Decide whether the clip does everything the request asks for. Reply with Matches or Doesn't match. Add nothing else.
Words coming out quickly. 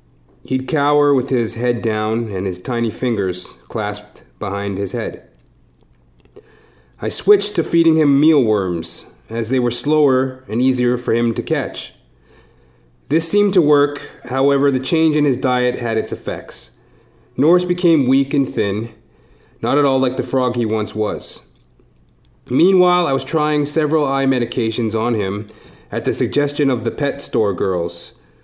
Doesn't match